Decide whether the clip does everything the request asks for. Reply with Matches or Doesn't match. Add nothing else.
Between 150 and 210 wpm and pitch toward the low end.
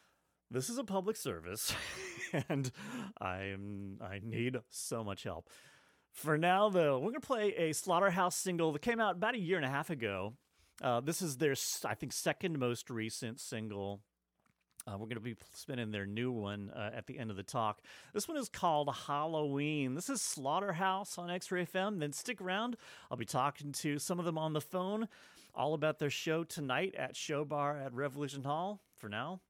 Doesn't match